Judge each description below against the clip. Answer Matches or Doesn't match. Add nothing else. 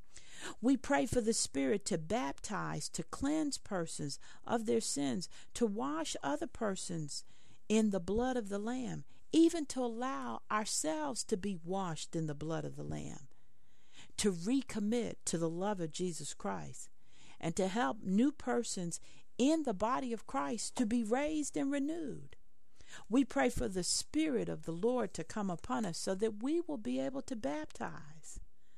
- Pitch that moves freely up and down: Matches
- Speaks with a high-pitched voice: Matches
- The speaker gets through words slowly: Doesn't match